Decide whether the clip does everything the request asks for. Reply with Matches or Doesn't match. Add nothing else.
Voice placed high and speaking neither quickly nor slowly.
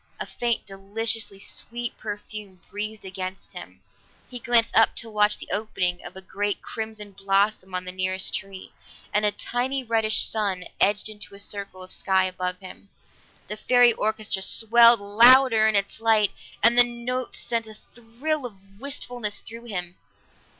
Matches